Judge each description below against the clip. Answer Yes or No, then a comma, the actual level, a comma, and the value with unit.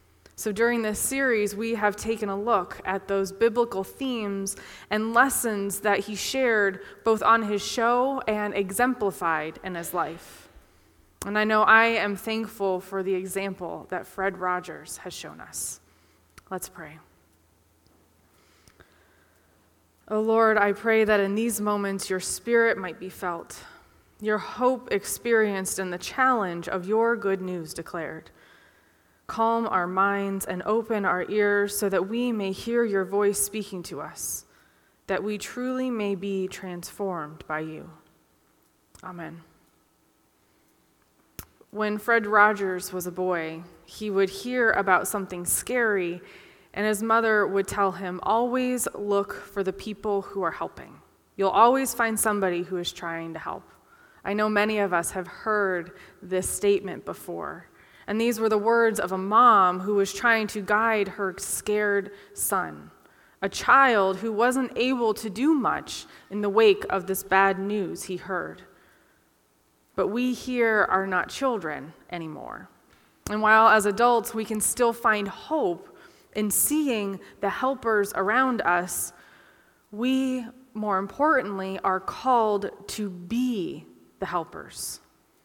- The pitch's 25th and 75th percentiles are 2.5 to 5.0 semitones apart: Yes, average, 3.3 semitones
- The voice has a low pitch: No, high, 205 Hz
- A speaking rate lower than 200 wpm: Yes, average, 145 wpm